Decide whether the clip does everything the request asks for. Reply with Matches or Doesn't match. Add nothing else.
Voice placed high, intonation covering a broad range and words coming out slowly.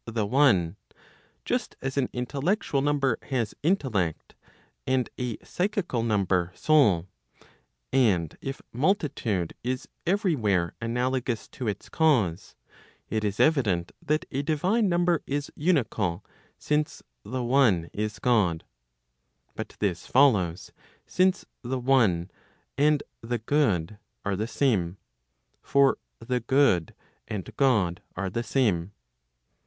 Doesn't match